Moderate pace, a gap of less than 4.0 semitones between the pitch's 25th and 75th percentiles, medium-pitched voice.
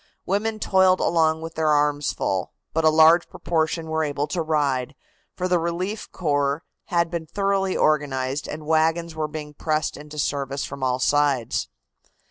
Yes: average, 160 wpm; average, 2.7 semitones; medium, 155 Hz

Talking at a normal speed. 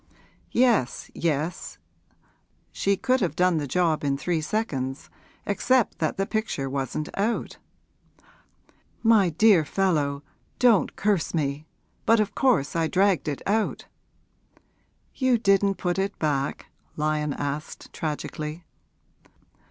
No: slow, 115 wpm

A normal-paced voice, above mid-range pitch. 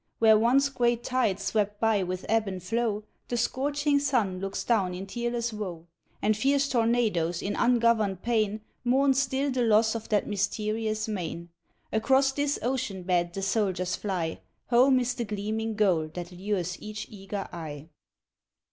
Yes: average, 155 wpm; high, 215 Hz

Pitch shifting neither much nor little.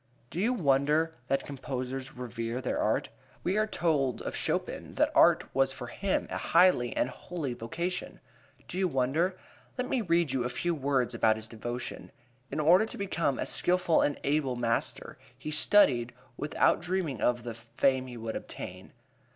No: wide, 5.9 semitones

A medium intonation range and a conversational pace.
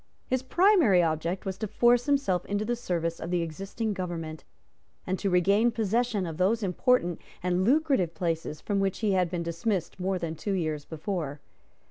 Yes: average, 4.6 semitones; average, 175 wpm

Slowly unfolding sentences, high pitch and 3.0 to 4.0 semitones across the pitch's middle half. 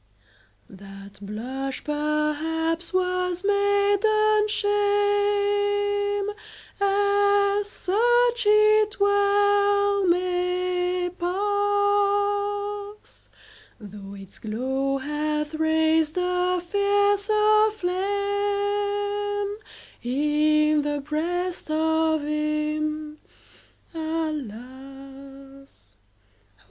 No: slow, 60 wpm; very high, 365 Hz; average, 5.2 semitones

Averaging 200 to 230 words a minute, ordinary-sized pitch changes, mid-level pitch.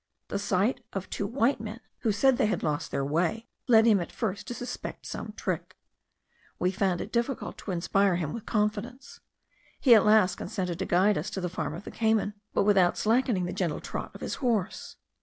No: fast, 205 wpm; average, 3.8 semitones; high, 205 Hz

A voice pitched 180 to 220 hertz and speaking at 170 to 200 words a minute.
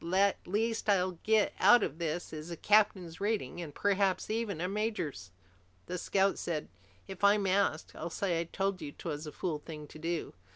Yes: medium, 185 Hz; average, 190 wpm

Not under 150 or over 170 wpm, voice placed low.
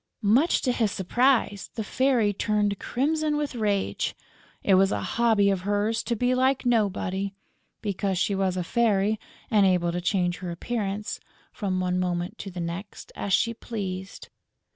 No: average, 165 wpm; high, 205 Hz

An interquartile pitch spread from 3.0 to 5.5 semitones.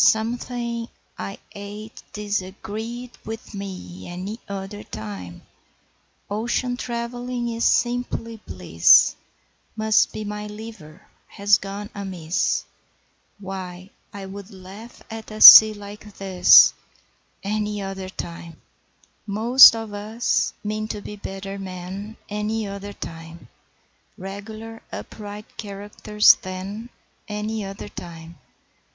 No: narrow, 2.4 semitones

